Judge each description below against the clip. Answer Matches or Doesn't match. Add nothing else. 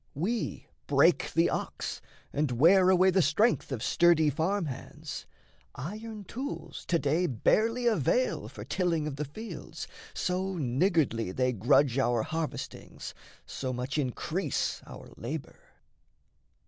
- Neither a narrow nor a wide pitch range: Doesn't match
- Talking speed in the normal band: Doesn't match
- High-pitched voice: Doesn't match